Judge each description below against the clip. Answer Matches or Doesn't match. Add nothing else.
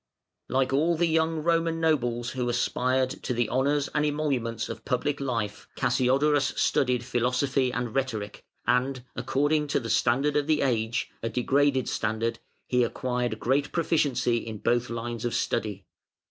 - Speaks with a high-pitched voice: Doesn't match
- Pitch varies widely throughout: Doesn't match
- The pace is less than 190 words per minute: Matches